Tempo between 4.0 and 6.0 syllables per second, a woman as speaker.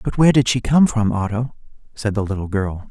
No: 5.8 syllables/s; male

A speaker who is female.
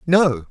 No: male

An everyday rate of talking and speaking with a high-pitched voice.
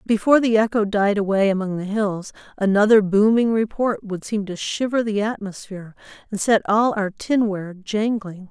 Yes: average, 160 wpm; high, 210 Hz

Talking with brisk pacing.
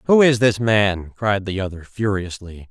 No: average, 175 wpm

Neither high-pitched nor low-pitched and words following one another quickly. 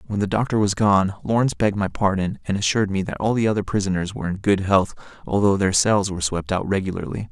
No: low, 100 Hz; fast, 230 wpm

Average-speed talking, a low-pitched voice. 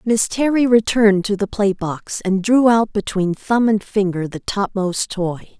No: average, 180 wpm; high, 205 Hz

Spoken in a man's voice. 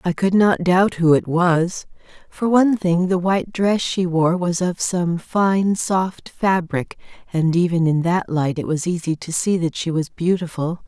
No: female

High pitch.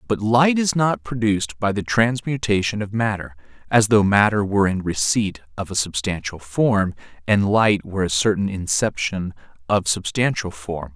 No: low, 105 Hz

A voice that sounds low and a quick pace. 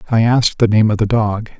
Yes: low, 110 Hz; fast, 265 wpm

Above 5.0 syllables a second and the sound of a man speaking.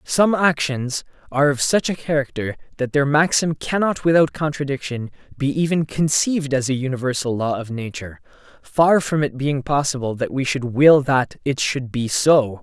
No: 4.9 syllables/s; male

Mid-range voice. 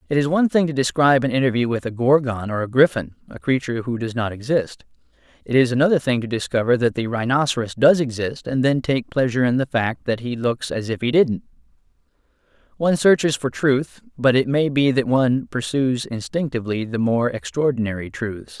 No: low, 130 Hz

